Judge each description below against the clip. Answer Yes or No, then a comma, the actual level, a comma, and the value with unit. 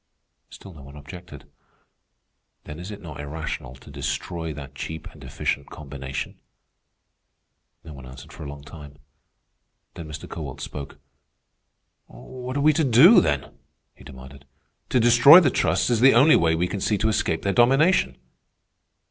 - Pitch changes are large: Yes, wide, 8.5 semitones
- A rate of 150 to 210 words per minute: Yes, average, 155 wpm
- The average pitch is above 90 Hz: No, very low, 80 Hz